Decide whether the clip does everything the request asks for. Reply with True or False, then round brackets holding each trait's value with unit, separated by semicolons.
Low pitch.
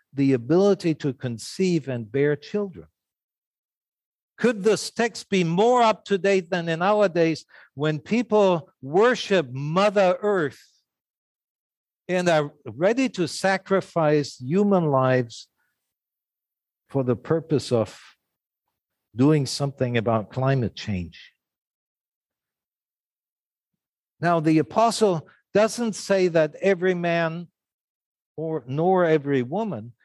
False (170 Hz)